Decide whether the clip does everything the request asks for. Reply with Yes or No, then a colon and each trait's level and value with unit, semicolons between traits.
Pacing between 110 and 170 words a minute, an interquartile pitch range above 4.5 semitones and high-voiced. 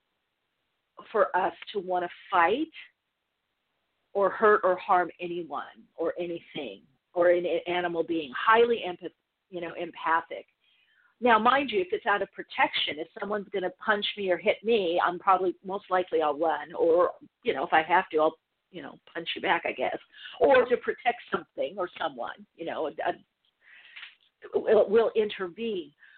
Yes: average, 160 wpm; average, 5.2 semitones; high, 195 Hz